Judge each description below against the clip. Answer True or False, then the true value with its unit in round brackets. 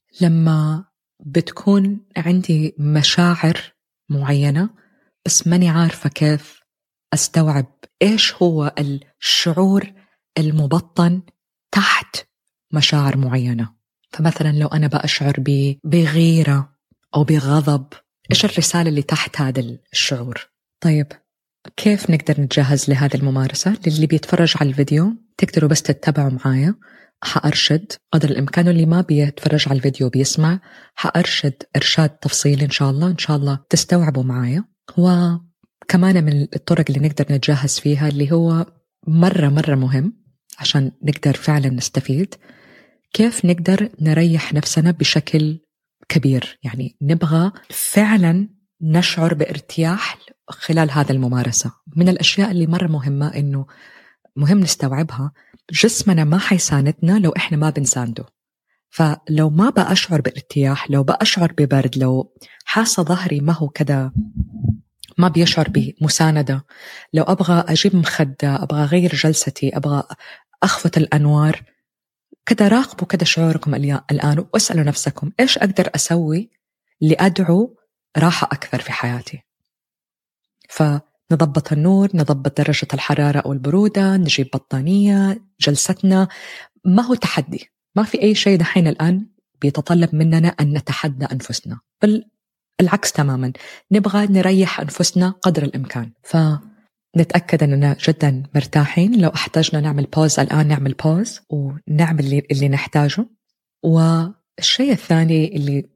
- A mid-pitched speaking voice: True (155 Hz)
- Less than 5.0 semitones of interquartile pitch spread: True (3.8 semitones)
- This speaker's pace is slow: False (115 wpm)